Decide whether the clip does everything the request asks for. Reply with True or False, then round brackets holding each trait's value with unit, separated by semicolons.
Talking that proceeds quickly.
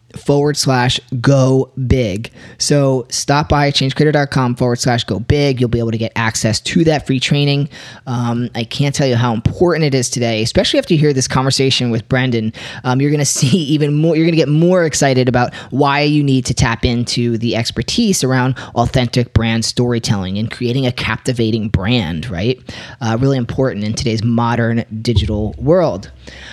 False (180 wpm)